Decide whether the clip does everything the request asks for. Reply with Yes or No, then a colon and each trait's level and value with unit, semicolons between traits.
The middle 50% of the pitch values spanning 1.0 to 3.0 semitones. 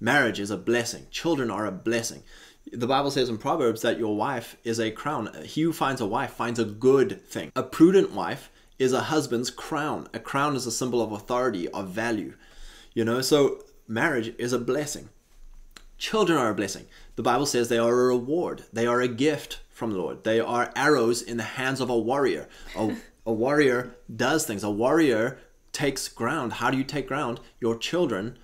Yes: average, 2.7 semitones